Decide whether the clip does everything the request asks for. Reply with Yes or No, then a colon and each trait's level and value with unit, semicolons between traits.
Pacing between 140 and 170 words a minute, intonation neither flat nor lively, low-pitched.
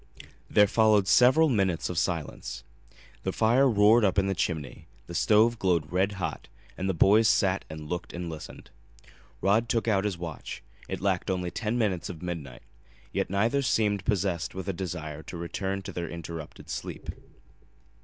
Yes: average, 165 wpm; average, 3.7 semitones; very low, 95 Hz